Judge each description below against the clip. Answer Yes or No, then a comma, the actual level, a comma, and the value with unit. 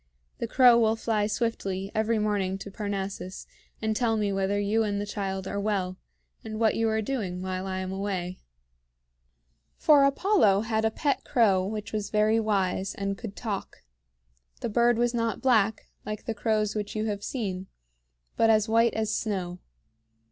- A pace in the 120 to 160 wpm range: No, average, 170 wpm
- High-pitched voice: Yes, high, 210 Hz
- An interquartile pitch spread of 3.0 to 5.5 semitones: No, narrow, 2.4 semitones